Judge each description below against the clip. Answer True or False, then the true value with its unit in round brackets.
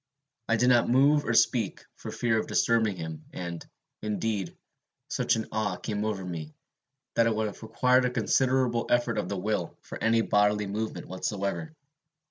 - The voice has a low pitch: True (110 Hz)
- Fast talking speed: False (170 wpm)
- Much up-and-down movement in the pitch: False (3.0 semitones)